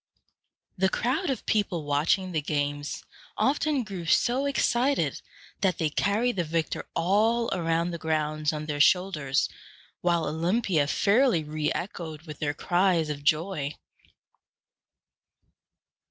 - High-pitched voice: No, medium, 170 Hz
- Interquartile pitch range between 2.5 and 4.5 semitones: No, average, 4.9 semitones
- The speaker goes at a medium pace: No, slow, 125 wpm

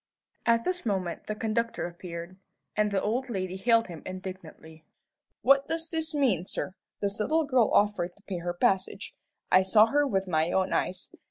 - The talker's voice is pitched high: Yes, high, 200 Hz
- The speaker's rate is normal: Yes, average, 175 wpm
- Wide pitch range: No, average, 4.2 semitones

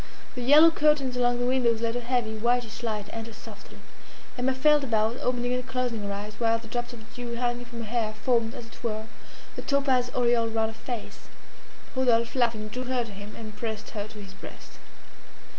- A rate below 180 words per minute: No, average, 200 wpm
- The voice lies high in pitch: Yes, high, 235 Hz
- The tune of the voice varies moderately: No, narrow, 2.1 semitones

